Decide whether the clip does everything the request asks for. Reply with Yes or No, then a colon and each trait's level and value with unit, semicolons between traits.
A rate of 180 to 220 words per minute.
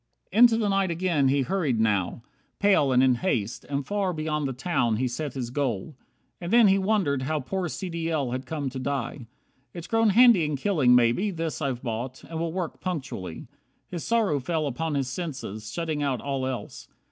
Yes: average, 200 wpm